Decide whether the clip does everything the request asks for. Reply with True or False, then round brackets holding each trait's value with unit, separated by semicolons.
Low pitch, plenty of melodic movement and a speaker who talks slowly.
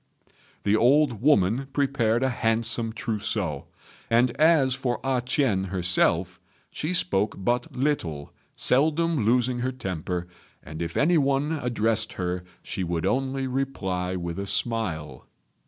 True (120 Hz; 6.1 semitones; 130 wpm)